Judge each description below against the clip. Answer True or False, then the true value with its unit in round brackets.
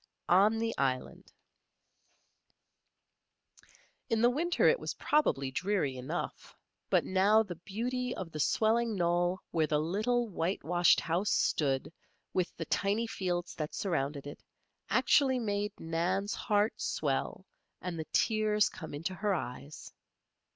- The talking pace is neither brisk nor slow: False (130 wpm)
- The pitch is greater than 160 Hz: True (185 Hz)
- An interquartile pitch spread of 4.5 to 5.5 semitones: True (5.0 semitones)